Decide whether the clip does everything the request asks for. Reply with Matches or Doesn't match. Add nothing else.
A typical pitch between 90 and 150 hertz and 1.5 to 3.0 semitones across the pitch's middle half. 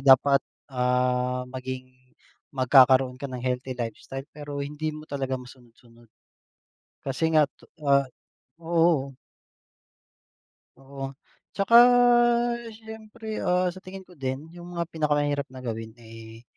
Doesn't match